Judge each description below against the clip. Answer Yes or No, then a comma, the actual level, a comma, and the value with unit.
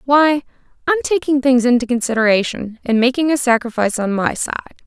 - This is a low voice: No, very high, 255 Hz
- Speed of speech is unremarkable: Yes, average, 160 wpm